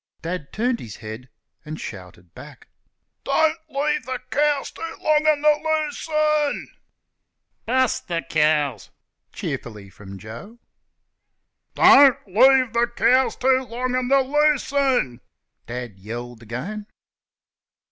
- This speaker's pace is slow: Yes, slow, 115 wpm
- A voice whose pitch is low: No, high, 245 Hz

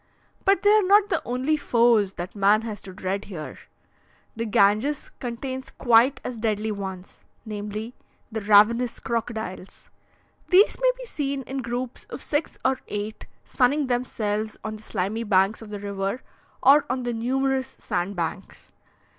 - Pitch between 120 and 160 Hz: No, high, 230 Hz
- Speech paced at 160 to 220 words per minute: No, average, 150 wpm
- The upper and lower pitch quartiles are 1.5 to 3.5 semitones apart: No, average, 4.2 semitones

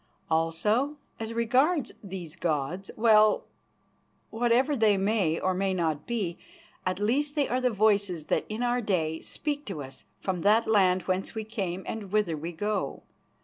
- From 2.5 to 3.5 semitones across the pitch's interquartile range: No, average, 4.3 semitones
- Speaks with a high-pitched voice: Yes, high, 205 Hz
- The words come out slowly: No, average, 160 wpm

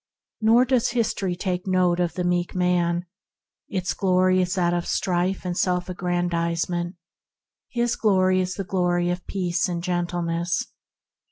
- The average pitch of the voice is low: No, medium, 180 Hz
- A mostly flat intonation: Yes, narrow, 1.1 semitones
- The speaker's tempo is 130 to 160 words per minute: Yes, average, 140 wpm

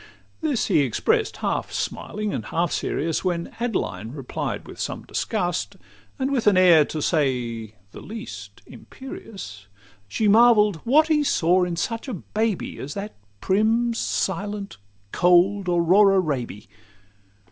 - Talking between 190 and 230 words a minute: No, slow, 135 wpm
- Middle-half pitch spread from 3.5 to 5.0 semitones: No, wide, 5.5 semitones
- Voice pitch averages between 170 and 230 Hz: Yes, high, 190 Hz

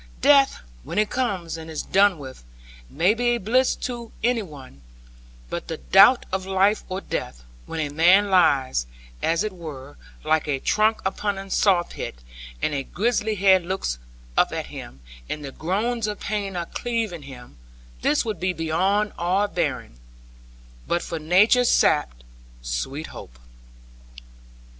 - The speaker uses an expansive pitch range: Yes, wide, 6.0 semitones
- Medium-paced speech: Yes, average, 150 wpm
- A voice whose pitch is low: No, medium, 185 Hz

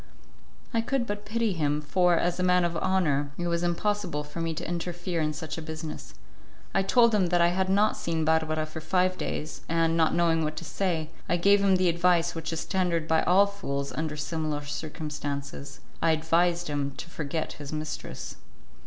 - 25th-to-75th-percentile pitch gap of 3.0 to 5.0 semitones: No, narrow, 2.6 semitones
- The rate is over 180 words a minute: Yes, average, 195 wpm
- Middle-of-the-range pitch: Yes, medium, 165 Hz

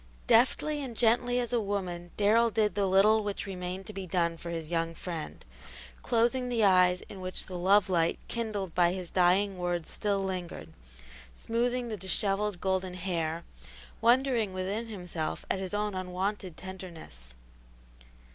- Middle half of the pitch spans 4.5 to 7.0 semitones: No, average, 3.3 semitones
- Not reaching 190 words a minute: Yes, average, 155 wpm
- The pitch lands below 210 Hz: Yes, high, 190 Hz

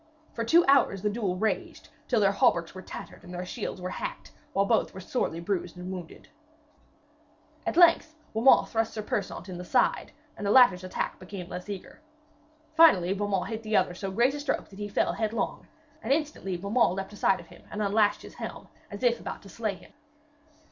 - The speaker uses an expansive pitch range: No, average, 3.8 semitones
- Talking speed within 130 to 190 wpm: No, average, 200 wpm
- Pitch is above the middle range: Yes, high, 205 Hz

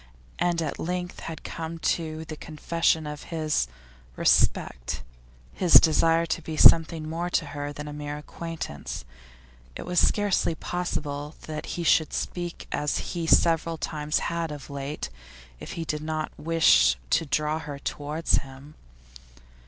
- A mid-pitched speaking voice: Yes, medium, 160 Hz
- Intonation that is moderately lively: No, narrow, 2.0 semitones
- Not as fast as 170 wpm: Yes, average, 145 wpm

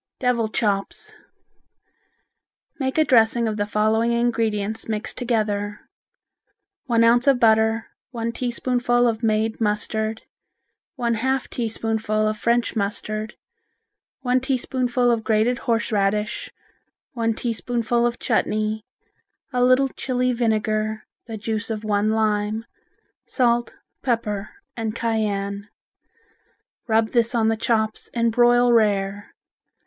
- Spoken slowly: Yes, slow, 115 wpm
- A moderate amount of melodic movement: No, narrow, 2.0 semitones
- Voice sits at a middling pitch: No, high, 225 Hz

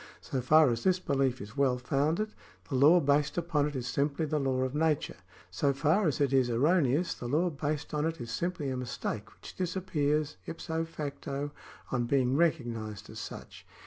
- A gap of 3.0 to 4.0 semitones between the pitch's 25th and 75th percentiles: Yes, average, 3.7 semitones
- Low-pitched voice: No, medium, 145 Hz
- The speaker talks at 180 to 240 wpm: Yes, average, 190 wpm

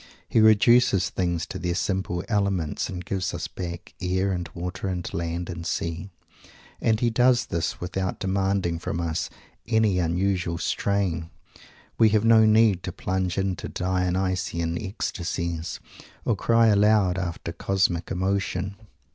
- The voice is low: Yes, very low, 95 Hz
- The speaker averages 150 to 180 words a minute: No, average, 140 wpm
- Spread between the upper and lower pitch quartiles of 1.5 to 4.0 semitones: Yes, narrow, 2.4 semitones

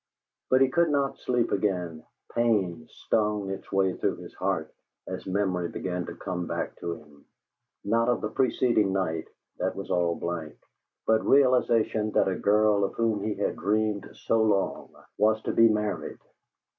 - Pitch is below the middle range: Yes, low, 105 Hz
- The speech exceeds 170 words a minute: No, average, 165 wpm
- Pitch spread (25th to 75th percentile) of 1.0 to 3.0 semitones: No, average, 3.7 semitones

